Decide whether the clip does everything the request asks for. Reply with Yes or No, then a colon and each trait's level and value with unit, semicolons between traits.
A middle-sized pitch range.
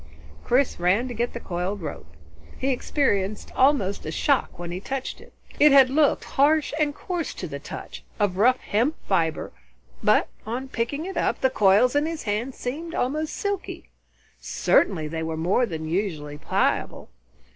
No: wide, 7.2 semitones